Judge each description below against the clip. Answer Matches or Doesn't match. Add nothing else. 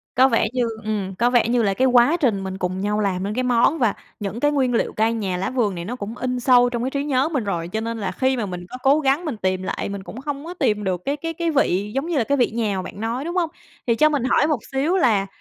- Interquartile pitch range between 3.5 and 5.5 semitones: Matches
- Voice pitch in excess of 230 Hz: Matches